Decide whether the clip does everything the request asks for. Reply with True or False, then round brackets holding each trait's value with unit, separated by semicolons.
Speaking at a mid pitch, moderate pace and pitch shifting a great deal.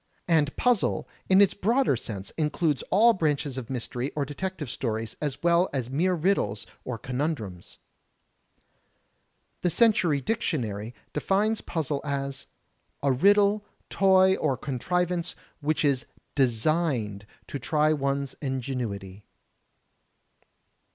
False (145 Hz; 115 wpm; 6.0 semitones)